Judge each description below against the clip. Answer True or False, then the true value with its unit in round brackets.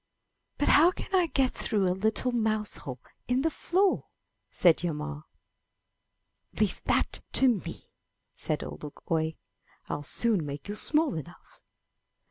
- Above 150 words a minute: False (145 wpm)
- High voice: True (210 Hz)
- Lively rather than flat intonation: True (9.0 semitones)